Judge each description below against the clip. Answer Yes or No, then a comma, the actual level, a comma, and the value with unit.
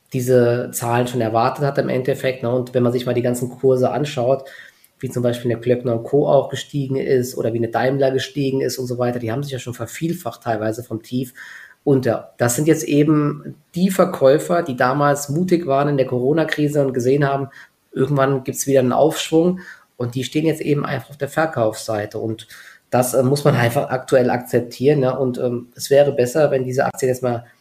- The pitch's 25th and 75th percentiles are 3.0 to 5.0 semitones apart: No, narrow, 2.6 semitones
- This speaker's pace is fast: Yes, fast, 205 wpm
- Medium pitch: No, low, 130 Hz